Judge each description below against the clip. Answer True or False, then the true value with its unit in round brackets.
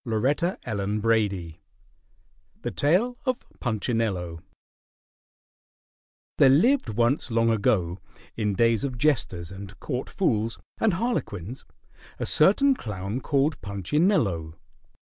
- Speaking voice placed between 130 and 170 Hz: False (115 Hz)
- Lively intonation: True (6.8 semitones)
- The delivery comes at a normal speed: False (100 wpm)